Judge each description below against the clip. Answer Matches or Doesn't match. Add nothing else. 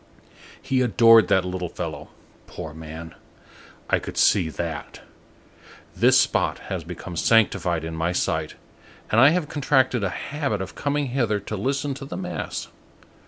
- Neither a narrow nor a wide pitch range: Doesn't match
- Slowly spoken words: Doesn't match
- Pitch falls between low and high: Doesn't match